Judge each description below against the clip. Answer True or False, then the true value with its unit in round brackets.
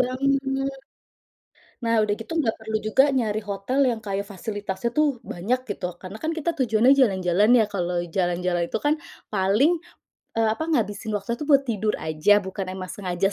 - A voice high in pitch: True (215 Hz)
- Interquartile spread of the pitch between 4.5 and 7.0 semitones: True (5.3 semitones)